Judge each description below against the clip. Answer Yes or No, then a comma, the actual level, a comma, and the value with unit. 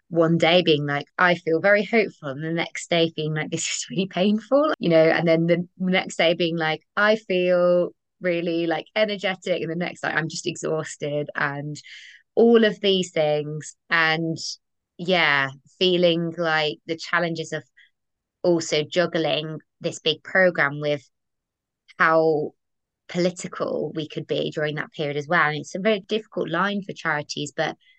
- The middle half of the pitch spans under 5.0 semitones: Yes, average, 2.8 semitones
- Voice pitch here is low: No, medium, 165 Hz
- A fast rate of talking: No, average, 165 wpm